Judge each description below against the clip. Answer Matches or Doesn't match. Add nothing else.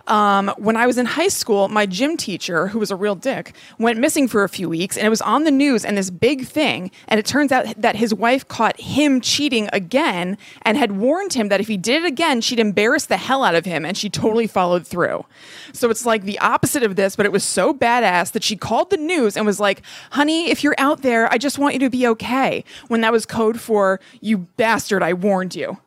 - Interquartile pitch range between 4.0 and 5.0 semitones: Matches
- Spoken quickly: Matches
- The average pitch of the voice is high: Matches